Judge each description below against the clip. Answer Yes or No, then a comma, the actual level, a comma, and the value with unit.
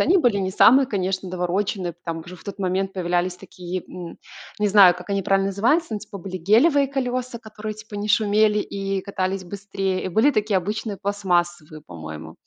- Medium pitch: No, high, 195 Hz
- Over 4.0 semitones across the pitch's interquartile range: No, average, 2.8 semitones